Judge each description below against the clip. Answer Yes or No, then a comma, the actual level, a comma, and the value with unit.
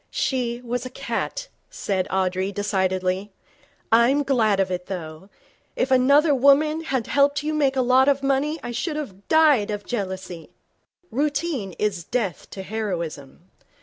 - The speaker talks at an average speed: Yes, average, 150 wpm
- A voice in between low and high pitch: No, high, 235 Hz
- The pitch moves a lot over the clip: Yes, wide, 6.7 semitones